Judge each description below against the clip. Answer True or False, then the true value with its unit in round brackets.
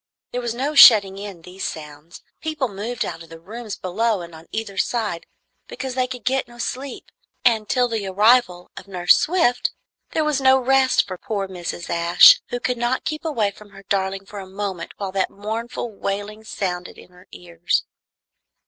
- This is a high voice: True (205 Hz)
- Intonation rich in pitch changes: False (4.8 semitones)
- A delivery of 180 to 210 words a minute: True (185 wpm)